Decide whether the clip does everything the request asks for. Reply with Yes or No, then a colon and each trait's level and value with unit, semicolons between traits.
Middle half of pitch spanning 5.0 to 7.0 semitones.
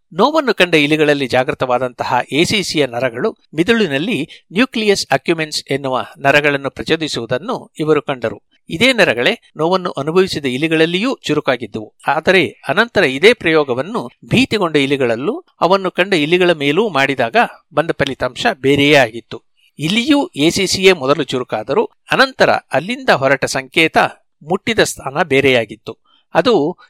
Yes: average, 5.3 semitones